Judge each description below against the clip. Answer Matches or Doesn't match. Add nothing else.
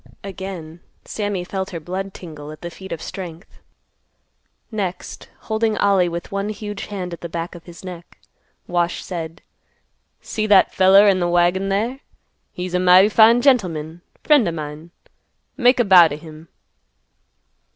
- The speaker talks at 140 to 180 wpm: Matches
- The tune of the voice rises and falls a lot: Doesn't match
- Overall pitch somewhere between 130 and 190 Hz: Matches